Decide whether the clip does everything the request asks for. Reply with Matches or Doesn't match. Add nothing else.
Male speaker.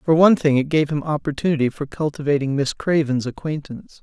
Matches